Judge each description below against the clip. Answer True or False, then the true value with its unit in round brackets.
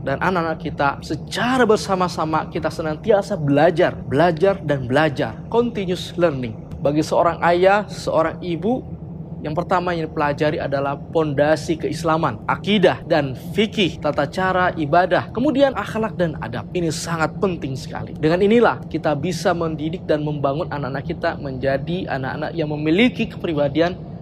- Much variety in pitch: False (3.0 semitones)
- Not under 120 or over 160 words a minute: True (130 wpm)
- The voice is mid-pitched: True (165 Hz)